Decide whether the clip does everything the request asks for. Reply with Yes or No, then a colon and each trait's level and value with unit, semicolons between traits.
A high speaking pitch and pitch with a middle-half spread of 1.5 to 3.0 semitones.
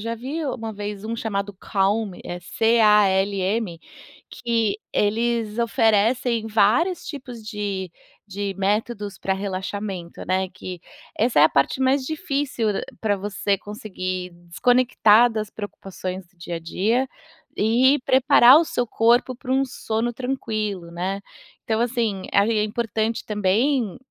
No: high, 215 Hz; average, 3.4 semitones